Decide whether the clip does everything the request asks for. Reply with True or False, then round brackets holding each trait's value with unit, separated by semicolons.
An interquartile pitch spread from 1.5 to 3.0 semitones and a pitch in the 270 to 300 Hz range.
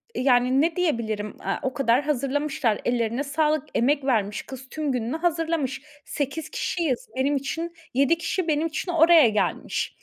False (4.3 semitones; 280 Hz)